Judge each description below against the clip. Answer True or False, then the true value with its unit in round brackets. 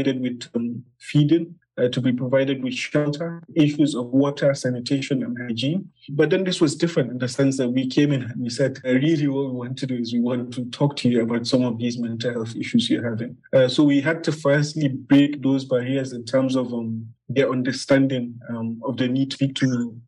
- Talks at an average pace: False (225 wpm)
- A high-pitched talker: False (130 Hz)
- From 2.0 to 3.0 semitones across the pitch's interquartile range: True (2.6 semitones)